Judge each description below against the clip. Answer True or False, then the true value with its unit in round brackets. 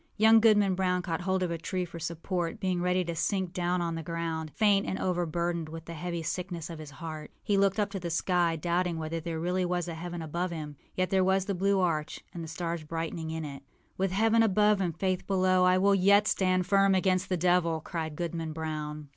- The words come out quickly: True (225 wpm)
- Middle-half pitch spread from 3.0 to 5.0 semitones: False (2.4 semitones)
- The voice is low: False (175 Hz)